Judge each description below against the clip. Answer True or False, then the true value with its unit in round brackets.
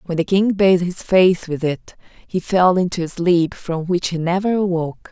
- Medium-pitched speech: True (180 Hz)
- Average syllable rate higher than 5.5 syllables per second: False (4.9 syllables/s)